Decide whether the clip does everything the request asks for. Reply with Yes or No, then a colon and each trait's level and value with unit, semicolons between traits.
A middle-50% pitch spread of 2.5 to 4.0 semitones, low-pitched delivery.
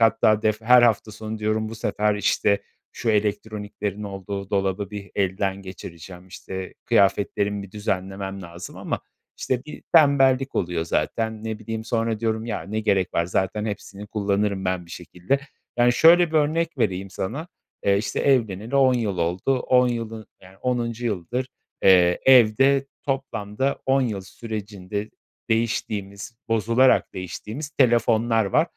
Yes: average, 3.3 semitones; low, 105 Hz